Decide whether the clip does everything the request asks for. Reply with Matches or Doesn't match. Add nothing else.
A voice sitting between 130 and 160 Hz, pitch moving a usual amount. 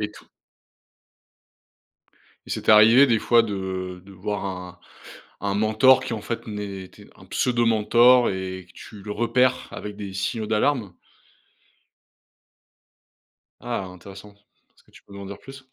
Doesn't match